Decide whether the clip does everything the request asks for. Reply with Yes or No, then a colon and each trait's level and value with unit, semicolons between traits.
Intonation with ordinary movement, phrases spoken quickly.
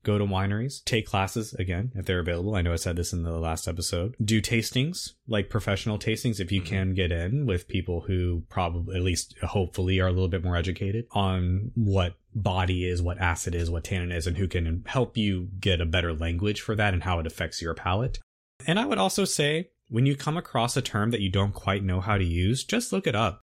Yes: average, 3.8 semitones; fast, 230 wpm